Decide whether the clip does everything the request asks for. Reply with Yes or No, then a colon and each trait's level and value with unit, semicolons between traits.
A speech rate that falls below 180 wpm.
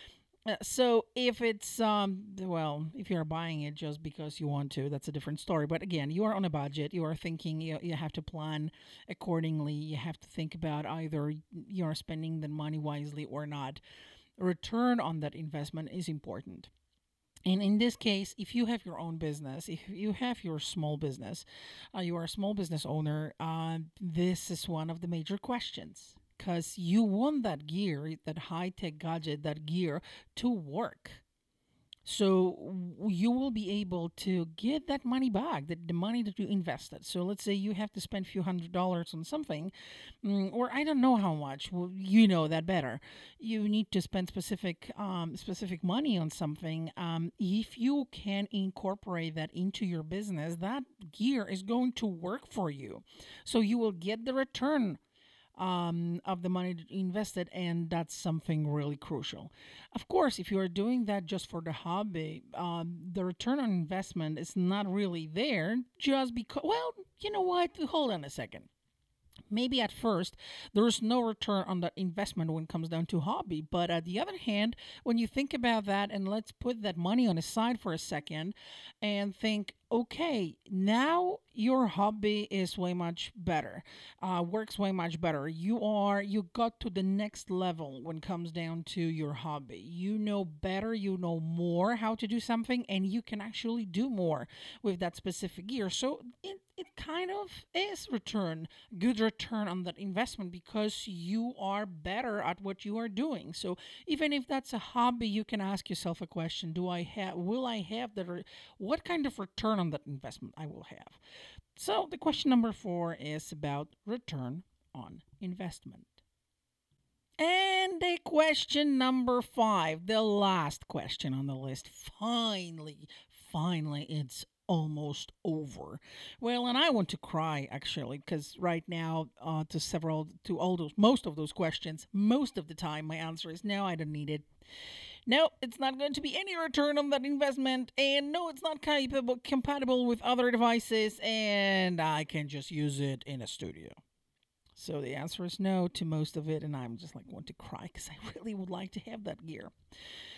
No: average, 185 wpm